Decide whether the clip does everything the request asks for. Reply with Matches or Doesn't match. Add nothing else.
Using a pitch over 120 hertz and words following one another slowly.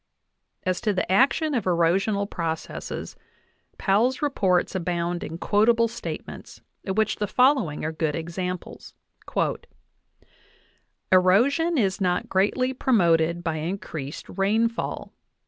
Matches